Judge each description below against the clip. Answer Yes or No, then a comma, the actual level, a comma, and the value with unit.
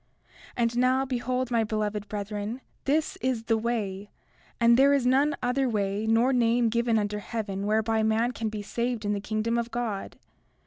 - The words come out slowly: No, average, 180 wpm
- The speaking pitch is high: Yes, high, 230 Hz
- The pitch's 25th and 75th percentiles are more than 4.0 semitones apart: No, narrow, 2.5 semitones